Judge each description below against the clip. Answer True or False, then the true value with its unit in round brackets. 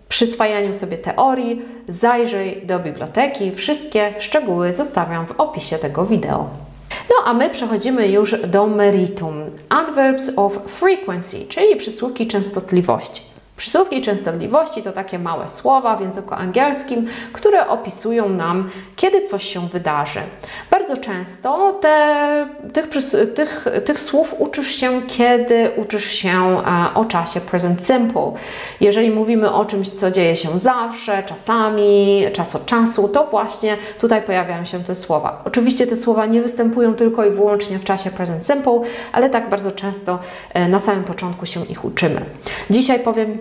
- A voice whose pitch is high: True (210 Hz)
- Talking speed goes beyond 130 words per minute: True (140 wpm)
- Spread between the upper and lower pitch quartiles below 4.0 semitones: False (4.4 semitones)